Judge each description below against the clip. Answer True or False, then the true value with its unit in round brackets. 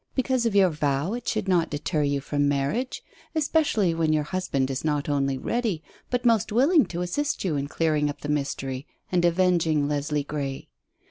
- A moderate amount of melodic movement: False (6.1 semitones)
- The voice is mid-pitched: True (160 Hz)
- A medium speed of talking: True (185 wpm)